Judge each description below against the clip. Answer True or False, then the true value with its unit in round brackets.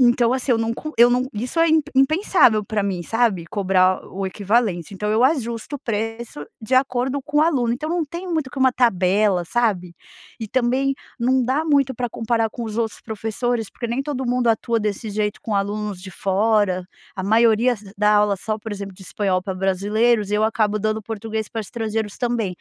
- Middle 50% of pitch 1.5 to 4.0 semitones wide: True (3.3 semitones)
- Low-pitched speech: False (225 Hz)